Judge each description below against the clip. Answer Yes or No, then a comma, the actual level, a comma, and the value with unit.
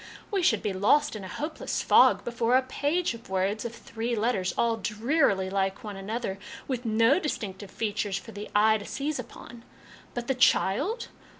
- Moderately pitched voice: No, high, 225 Hz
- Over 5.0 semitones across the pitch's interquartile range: No, average, 4.2 semitones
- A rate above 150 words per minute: Yes, average, 180 wpm